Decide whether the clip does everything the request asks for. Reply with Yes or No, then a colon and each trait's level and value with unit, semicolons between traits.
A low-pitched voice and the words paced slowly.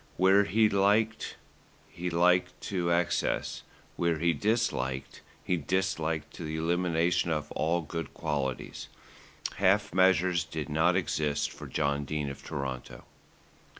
Yes: very low, 85 Hz; slow, 125 wpm